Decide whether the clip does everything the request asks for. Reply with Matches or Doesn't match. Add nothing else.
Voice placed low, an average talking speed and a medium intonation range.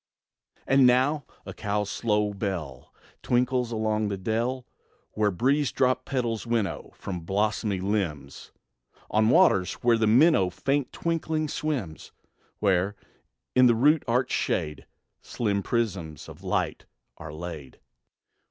Doesn't match